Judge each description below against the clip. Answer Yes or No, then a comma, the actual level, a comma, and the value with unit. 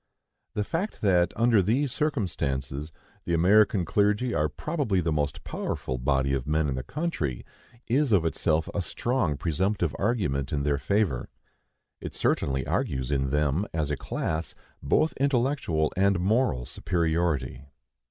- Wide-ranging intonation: Yes, wide, 7.0 semitones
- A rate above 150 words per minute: No, average, 145 wpm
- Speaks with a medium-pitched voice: No, very low, 85 Hz